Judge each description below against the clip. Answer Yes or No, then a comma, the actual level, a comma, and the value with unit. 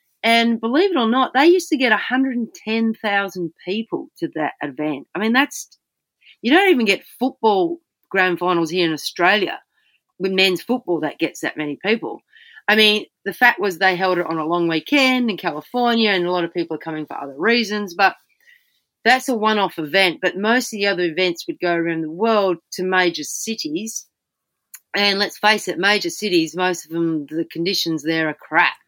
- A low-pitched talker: No, high, 200 Hz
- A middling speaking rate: Yes, average, 195 wpm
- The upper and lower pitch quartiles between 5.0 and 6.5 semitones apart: Yes, wide, 5.6 semitones